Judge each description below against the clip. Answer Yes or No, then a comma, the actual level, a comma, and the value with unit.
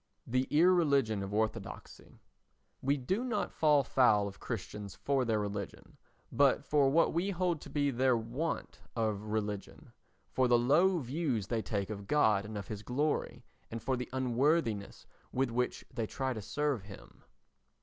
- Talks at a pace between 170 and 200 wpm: No, average, 160 wpm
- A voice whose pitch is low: Yes, low, 125 Hz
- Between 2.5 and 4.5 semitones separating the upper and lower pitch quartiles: No, wide, 5.4 semitones